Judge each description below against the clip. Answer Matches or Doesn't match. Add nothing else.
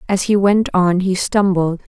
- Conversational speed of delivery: Matches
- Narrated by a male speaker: Doesn't match